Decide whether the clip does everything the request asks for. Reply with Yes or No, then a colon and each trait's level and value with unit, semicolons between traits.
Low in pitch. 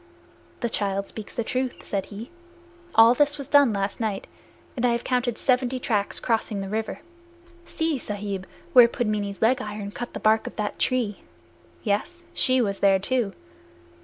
No: high, 225 Hz